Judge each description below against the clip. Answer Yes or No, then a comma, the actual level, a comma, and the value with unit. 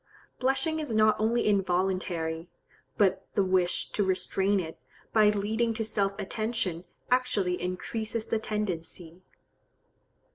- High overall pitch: Yes, high, 200 Hz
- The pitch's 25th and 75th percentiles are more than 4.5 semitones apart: No, average, 3.2 semitones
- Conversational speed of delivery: No, slow, 115 wpm